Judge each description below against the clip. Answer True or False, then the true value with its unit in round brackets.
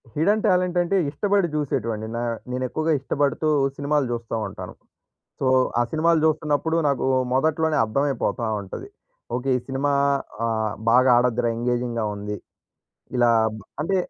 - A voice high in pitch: False (140 Hz)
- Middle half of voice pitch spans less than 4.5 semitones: False (4.8 semitones)